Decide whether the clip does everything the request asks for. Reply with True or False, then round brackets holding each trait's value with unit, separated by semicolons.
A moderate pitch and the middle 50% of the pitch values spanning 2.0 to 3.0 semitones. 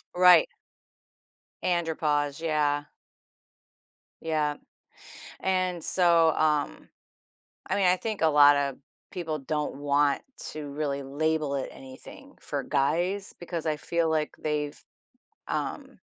True (155 Hz; 2.7 semitones)